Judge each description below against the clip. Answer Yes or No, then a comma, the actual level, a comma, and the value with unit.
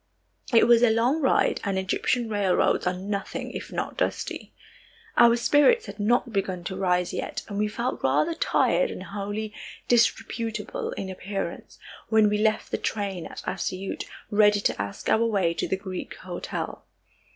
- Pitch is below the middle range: No, high, 210 Hz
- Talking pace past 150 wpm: Yes, average, 165 wpm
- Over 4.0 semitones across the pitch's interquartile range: No, average, 3.3 semitones